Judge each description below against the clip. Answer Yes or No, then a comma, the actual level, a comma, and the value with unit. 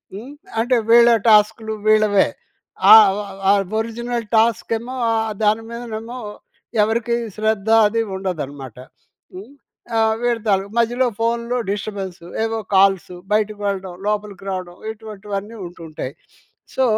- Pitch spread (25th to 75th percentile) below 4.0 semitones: Yes, average, 2.8 semitones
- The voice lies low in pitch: No, high, 215 Hz